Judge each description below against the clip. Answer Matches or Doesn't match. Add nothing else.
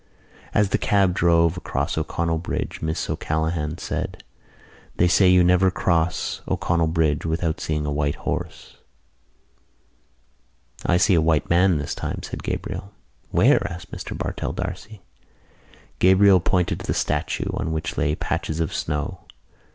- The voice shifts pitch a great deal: Doesn't match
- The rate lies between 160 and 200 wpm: Doesn't match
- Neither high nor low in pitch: Doesn't match